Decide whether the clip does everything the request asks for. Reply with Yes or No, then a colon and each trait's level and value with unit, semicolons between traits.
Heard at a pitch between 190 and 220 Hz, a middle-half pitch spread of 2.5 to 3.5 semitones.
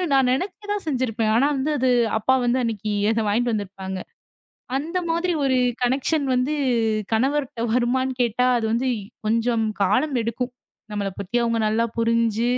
No: high, 240 Hz; average, 2.9 semitones